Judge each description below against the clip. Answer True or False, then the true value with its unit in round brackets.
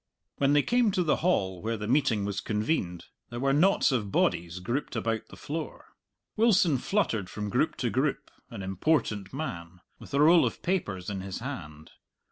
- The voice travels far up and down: True (7.8 semitones)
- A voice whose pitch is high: False (115 Hz)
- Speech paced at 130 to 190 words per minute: True (180 wpm)